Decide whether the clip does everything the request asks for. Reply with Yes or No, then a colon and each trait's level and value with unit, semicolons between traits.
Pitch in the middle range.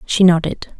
Yes: medium, 175 Hz